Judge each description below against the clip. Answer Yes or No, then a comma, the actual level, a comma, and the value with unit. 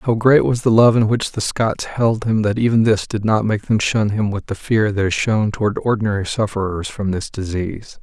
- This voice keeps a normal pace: No, fast, 240 wpm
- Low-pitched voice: Yes, low, 105 Hz